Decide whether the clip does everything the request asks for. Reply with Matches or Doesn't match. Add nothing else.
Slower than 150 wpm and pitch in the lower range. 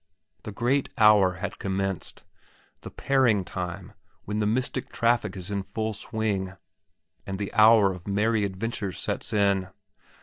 Matches